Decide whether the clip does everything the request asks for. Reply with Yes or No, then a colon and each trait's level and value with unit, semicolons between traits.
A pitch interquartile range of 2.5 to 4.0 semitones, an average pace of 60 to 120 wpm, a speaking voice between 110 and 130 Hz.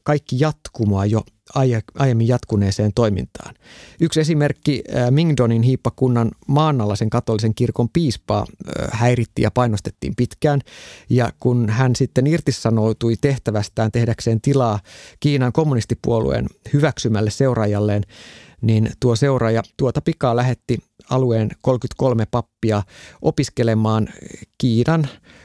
Yes: average, 3.5 semitones; average, 100 wpm; low, 120 Hz